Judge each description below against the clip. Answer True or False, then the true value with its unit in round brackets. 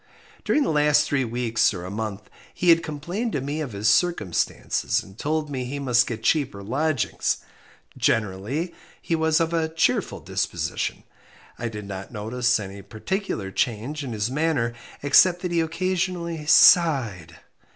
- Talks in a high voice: False (140 Hz)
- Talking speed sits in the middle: True (155 wpm)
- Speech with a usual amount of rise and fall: False (6.9 semitones)